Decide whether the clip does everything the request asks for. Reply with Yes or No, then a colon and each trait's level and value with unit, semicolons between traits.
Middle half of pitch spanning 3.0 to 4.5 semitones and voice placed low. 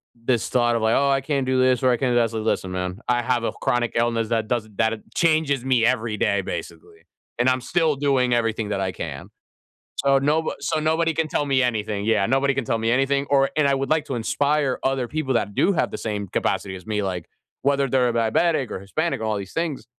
Yes: average, 3.8 semitones; low, 125 Hz